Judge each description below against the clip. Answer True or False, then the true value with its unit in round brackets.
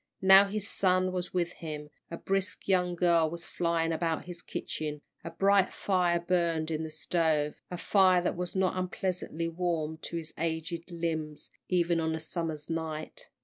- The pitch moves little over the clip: True (2.2 semitones)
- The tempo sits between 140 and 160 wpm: False (170 wpm)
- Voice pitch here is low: False (170 Hz)